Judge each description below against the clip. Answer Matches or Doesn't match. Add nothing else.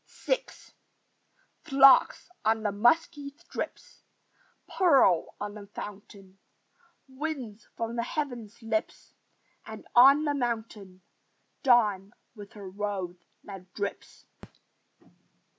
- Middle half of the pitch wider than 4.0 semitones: Matches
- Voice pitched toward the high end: Matches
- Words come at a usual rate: Doesn't match